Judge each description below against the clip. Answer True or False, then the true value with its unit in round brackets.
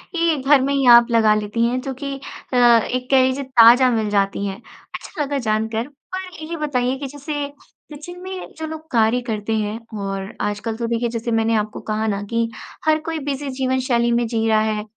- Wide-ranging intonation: False (4.2 semitones)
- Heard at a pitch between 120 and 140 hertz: False (240 Hz)